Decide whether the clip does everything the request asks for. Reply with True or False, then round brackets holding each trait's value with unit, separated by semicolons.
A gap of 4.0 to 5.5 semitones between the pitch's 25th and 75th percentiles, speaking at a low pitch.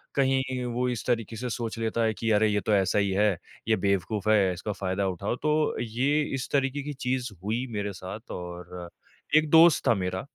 True (4.4 semitones; 110 Hz)